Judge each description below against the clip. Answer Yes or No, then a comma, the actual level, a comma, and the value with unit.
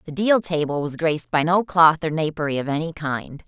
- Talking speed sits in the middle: No, fast, 225 wpm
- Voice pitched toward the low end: No, medium, 160 Hz